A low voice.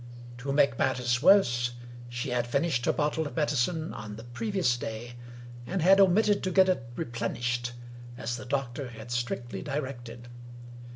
Yes: low, 125 Hz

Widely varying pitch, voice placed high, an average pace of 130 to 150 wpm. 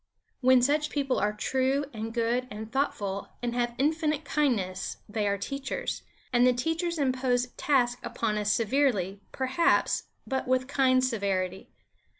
No: average, 4.3 semitones; very high, 250 Hz; average, 145 wpm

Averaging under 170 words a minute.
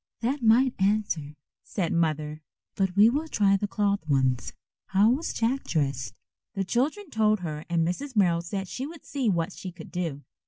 No: average, 180 wpm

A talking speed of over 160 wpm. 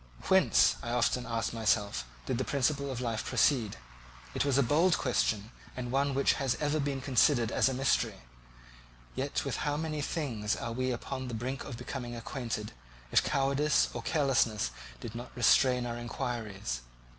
Yes: average, 170 wpm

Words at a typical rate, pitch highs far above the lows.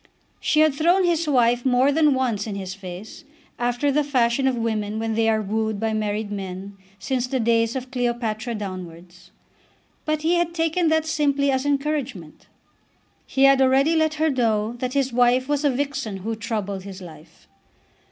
No: average, 175 wpm; average, 4.9 semitones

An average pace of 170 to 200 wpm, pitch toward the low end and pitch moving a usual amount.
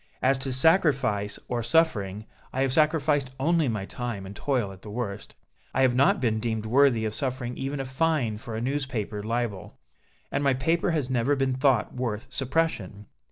Yes: average, 180 wpm; low, 130 Hz; average, 4.1 semitones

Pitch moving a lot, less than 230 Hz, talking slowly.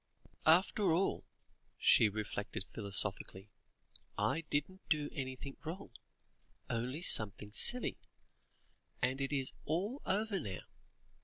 Yes: wide, 8.7 semitones; medium, 140 Hz; slow, 100 wpm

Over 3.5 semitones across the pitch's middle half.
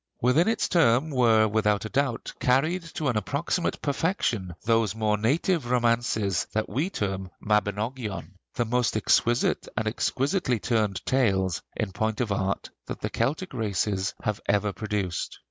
Yes: average, 3.9 semitones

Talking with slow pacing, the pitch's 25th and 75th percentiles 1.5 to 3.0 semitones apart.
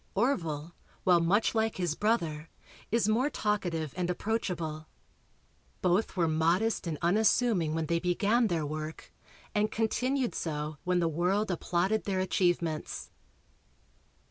No: slow, 125 wpm; average, 4.8 semitones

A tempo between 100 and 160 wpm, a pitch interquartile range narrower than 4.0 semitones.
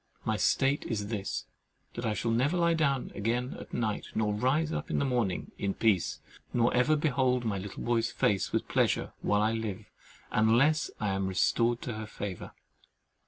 No: average, 175 wpm; average, 3.6 semitones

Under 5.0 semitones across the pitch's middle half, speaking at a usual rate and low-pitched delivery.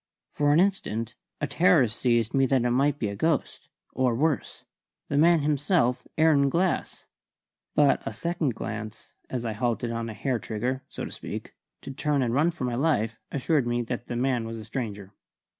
Yes: average, 4.2 semitones; average, 190 wpm; low, 130 Hz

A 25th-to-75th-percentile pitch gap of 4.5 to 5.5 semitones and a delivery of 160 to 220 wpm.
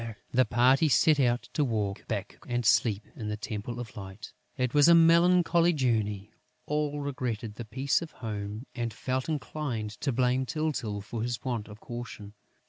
Yes: average, 4.9 semitones; average, 170 wpm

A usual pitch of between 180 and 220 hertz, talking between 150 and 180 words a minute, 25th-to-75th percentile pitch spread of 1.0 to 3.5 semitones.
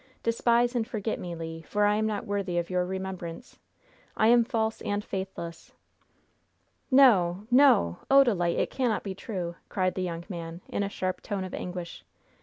No: high, 190 Hz; average, 170 wpm; average, 4.3 semitones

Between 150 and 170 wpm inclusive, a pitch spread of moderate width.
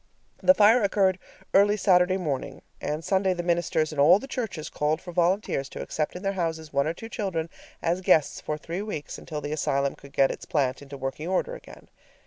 No: fast, 205 wpm; average, 4.2 semitones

